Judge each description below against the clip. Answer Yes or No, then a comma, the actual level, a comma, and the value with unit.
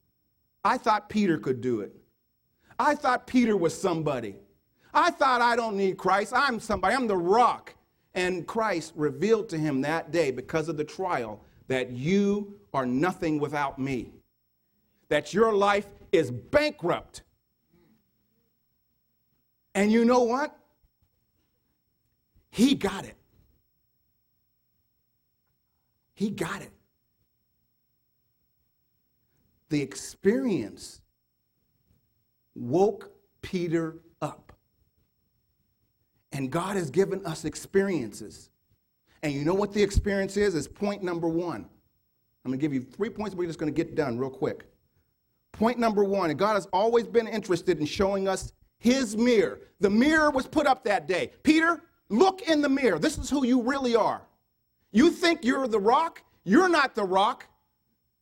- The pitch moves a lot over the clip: Yes, wide, 7.6 semitones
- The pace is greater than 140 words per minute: No, slow, 135 wpm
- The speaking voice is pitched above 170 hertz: Yes, high, 190 Hz